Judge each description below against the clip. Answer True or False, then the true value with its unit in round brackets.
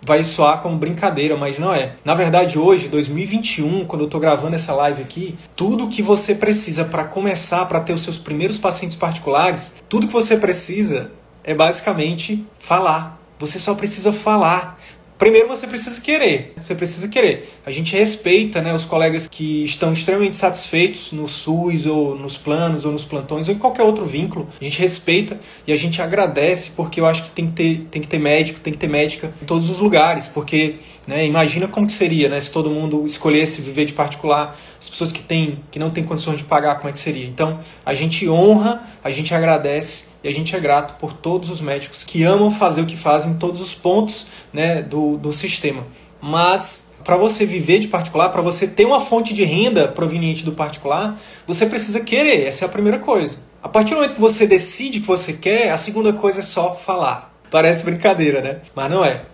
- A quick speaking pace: True (205 wpm)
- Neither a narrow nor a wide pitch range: True (4.0 semitones)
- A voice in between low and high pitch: True (165 Hz)